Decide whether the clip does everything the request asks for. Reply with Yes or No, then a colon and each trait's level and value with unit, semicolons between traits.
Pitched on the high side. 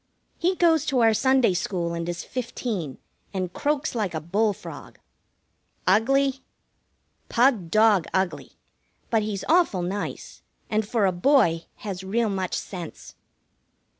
Yes: high, 210 Hz